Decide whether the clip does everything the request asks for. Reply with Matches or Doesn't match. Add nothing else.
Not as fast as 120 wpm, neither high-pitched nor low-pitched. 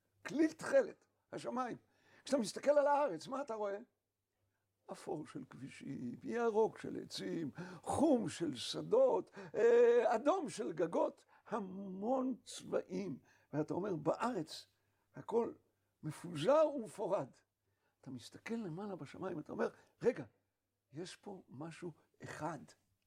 Doesn't match